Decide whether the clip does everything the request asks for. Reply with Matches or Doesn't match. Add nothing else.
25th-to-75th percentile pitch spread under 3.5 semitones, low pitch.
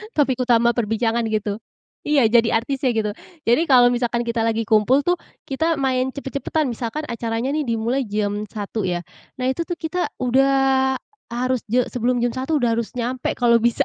Doesn't match